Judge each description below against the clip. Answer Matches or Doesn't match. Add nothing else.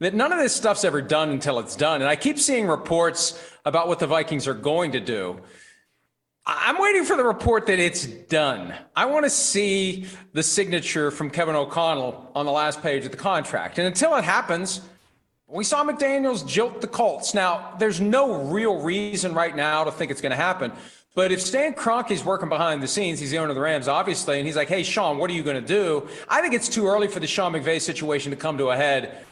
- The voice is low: Doesn't match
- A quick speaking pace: Matches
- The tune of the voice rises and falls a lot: Matches